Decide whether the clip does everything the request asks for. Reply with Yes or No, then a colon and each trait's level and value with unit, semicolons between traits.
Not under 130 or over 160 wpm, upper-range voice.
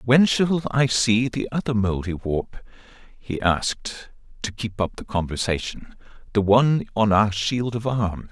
No: average, 145 wpm; low, 110 Hz